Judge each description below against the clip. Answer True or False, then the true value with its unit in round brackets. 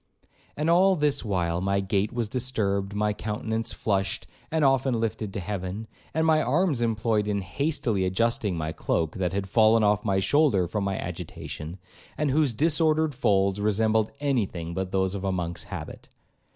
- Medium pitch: False (105 Hz)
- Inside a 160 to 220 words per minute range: True (170 wpm)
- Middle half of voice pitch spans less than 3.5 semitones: False (5.3 semitones)